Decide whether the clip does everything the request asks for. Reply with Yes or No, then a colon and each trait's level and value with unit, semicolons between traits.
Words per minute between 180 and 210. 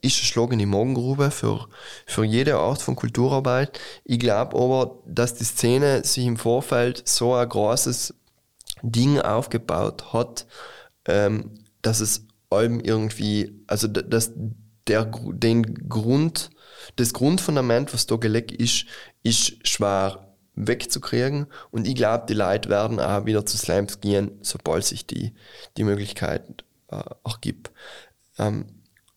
No: slow, 125 wpm